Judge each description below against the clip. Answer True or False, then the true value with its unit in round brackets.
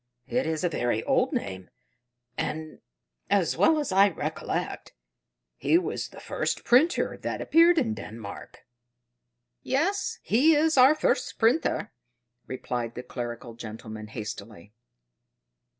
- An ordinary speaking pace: False (120 wpm)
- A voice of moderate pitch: True (160 Hz)